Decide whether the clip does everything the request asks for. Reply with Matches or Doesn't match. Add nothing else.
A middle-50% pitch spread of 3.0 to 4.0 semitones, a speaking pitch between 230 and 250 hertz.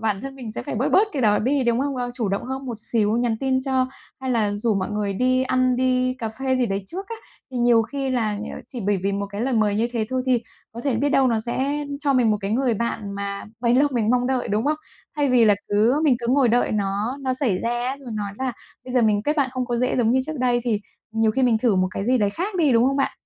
Matches